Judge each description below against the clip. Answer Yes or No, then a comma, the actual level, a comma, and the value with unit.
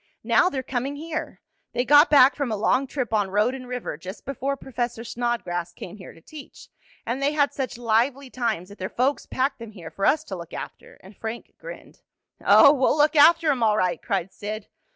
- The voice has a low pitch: No, high, 245 Hz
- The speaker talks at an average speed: No, fast, 210 wpm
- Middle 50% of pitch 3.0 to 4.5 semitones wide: No, average, 5.0 semitones